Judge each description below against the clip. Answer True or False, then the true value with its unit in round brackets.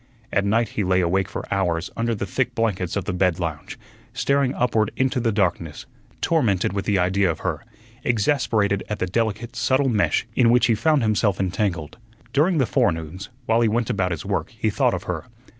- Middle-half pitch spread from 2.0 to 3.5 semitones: False (4.3 semitones)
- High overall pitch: False (105 Hz)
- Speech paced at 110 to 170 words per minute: False (195 wpm)